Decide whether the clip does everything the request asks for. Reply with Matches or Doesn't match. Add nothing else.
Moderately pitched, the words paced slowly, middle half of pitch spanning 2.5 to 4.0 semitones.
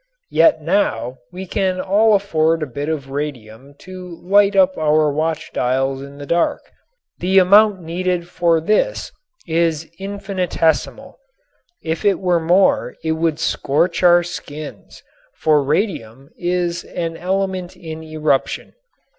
Matches